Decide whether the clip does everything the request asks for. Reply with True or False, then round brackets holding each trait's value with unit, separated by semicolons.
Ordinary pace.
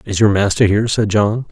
False (240 wpm)